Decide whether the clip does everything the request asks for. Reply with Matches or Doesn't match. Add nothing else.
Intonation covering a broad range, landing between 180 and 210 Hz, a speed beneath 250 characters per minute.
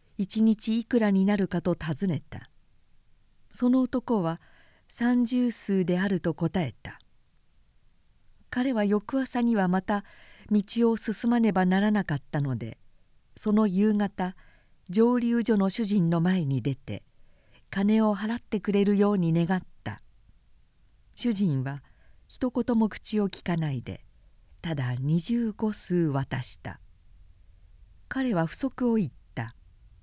Matches